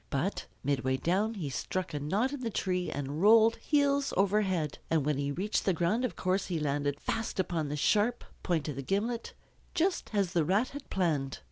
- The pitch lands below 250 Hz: Yes, medium, 185 Hz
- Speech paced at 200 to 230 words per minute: Yes, fast, 205 wpm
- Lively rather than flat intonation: Yes, wide, 6.6 semitones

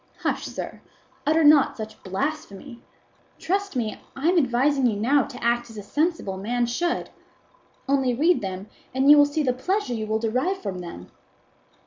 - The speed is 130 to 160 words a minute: No, average, 170 wpm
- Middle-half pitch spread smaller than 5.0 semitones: No, average, 5.3 semitones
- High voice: Yes, very high, 255 Hz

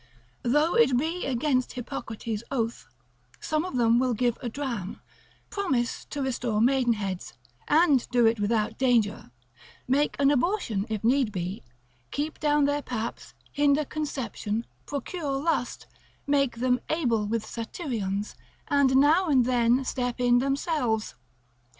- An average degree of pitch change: Yes, average, 3.9 semitones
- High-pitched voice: Yes, very high, 250 Hz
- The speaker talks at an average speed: No, slow, 130 wpm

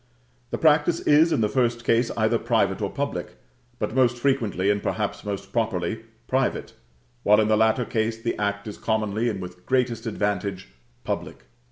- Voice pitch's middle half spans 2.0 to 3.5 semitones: Yes, average, 3.0 semitones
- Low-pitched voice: Yes, low, 110 Hz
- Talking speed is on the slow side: No, average, 170 wpm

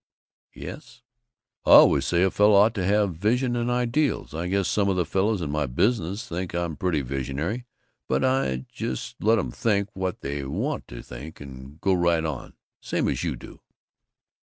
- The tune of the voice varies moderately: No, wide, 6.1 semitones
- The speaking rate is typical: Yes, average, 185 wpm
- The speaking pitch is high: No, very low, 90 Hz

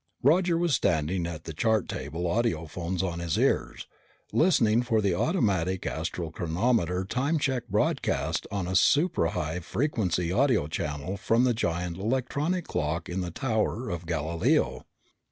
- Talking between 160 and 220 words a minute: No, average, 140 wpm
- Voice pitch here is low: Yes, very low, 95 Hz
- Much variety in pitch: Yes, wide, 6.5 semitones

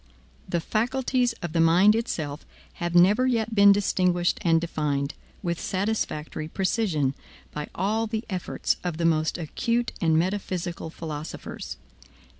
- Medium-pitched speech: Yes, medium, 175 Hz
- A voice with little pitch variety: No, average, 4.9 semitones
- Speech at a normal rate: No, slow, 130 wpm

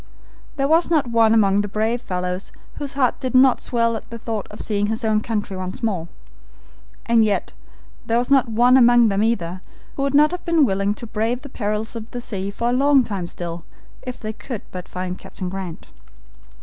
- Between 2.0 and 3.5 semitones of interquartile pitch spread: No, average, 3.9 semitones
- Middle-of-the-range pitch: No, high, 225 Hz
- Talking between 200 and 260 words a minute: Yes, fast, 205 wpm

